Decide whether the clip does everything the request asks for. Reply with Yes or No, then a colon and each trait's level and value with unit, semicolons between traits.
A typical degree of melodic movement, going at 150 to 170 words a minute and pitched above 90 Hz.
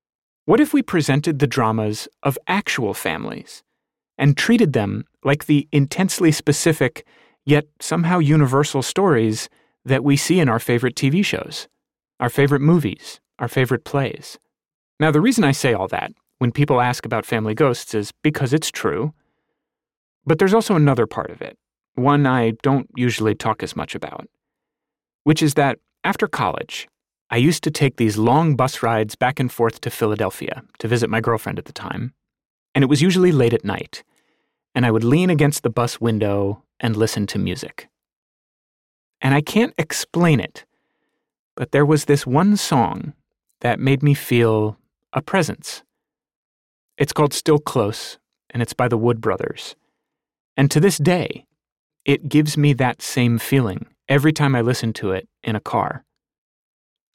Yes: average, 4.4 semitones; average, 165 wpm; low, 135 Hz